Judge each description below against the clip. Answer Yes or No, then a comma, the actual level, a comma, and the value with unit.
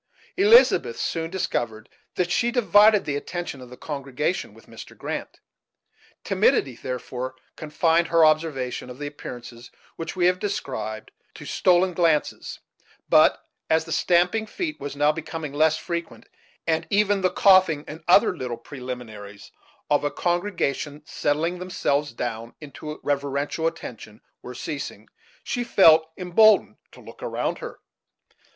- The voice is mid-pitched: Yes, medium, 160 Hz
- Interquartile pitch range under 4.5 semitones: No, average, 4.8 semitones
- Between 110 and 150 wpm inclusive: Yes, average, 140 wpm